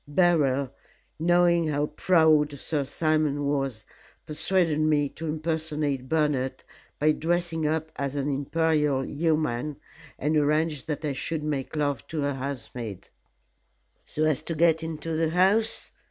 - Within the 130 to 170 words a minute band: Yes, average, 140 wpm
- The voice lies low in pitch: No, medium, 150 Hz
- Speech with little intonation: Yes, narrow, 2.2 semitones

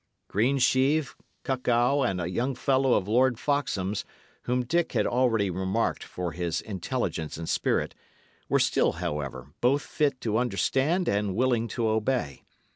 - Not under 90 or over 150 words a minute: Yes, average, 140 wpm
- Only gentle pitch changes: No, wide, 5.6 semitones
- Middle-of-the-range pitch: No, low, 120 Hz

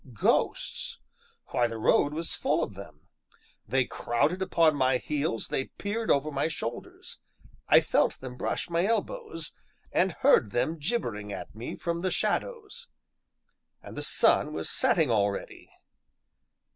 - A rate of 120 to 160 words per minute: Yes, average, 140 wpm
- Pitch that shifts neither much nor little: No, wide, 6.3 semitones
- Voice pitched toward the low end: No, medium, 145 Hz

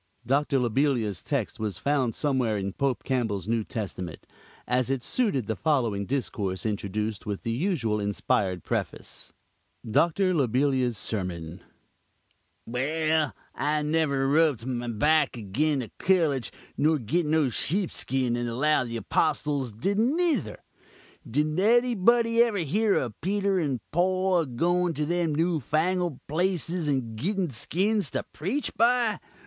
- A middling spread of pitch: No, wide, 7.0 semitones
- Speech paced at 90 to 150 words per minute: Yes, slow, 135 wpm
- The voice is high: No, medium, 140 Hz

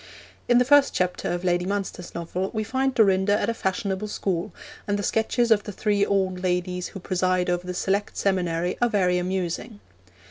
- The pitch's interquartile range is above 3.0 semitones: No, narrow, 2.5 semitones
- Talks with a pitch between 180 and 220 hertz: Yes, high, 190 Hz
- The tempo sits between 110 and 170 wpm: No, average, 185 wpm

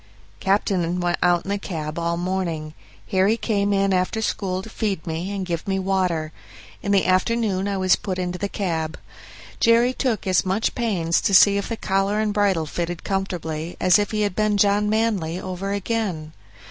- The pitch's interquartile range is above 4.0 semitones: No, narrow, 2.6 semitones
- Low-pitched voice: No, high, 190 Hz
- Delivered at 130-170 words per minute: No, average, 190 wpm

